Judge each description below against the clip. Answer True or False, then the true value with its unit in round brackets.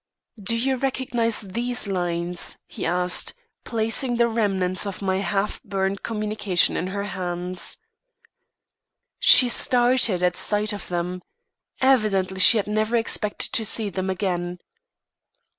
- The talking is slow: True (125 wpm)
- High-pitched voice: True (200 Hz)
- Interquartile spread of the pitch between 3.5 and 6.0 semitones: True (3.8 semitones)